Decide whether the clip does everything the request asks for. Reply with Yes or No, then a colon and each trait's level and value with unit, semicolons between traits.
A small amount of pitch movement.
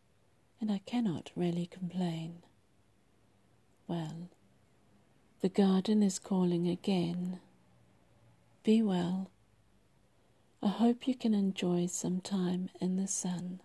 Yes: narrow, 2.3 semitones